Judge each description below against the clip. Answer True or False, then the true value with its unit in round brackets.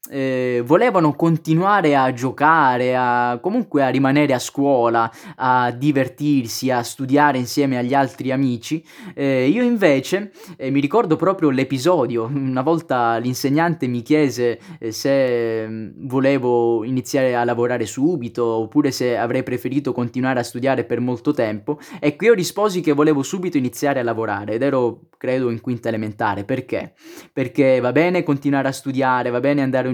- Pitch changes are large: False (3.3 semitones)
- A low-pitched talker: True (130 Hz)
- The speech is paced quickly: False (150 wpm)